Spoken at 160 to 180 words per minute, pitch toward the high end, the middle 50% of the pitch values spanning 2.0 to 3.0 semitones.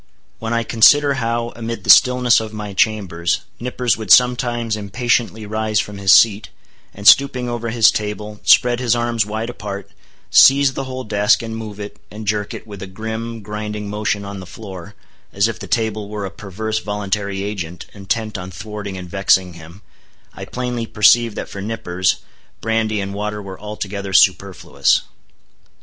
No: average, 170 wpm; low, 105 Hz; narrow, 2.4 semitones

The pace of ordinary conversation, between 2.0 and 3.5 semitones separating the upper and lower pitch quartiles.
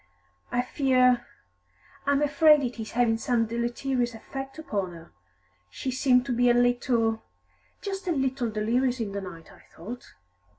Yes: average, 160 wpm; average, 2.9 semitones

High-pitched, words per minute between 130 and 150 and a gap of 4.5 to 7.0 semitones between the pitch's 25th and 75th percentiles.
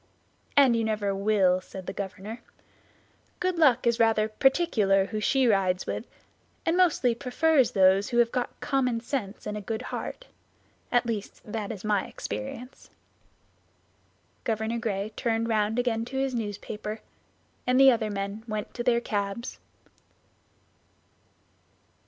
No: high, 225 Hz; average, 140 wpm; average, 3.2 semitones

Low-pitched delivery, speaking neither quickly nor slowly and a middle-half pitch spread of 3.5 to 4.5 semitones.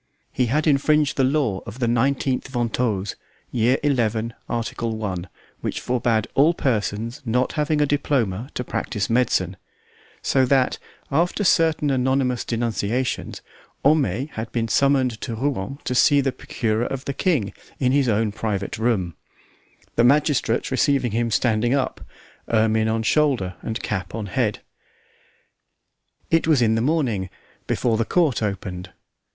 Yes: low, 120 Hz; average, 145 wpm; average, 3.9 semitones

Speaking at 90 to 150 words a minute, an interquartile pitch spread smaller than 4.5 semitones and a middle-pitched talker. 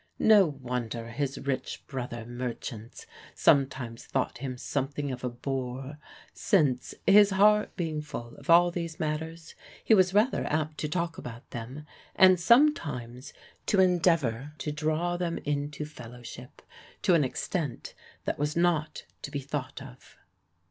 No: average, 140 wpm; average, 5.0 semitones; medium, 145 Hz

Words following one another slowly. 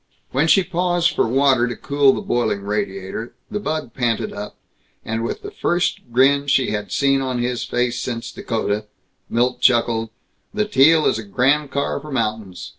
No: average, 175 wpm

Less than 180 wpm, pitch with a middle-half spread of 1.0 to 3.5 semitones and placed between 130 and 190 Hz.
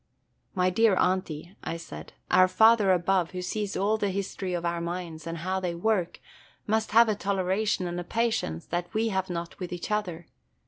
No: average, 190 wpm; average, 3.1 semitones; medium, 185 Hz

